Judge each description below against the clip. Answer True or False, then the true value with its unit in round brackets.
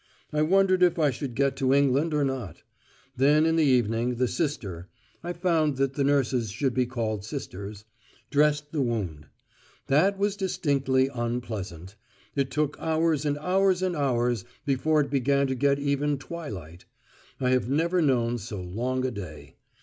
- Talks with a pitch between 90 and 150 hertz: True (135 Hz)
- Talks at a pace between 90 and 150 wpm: False (165 wpm)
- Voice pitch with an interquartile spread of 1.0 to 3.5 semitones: False (4.3 semitones)